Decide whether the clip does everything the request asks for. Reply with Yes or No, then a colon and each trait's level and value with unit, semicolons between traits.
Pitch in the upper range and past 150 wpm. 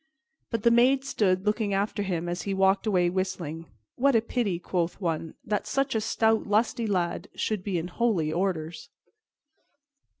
Yes: high, 195 Hz; average, 165 wpm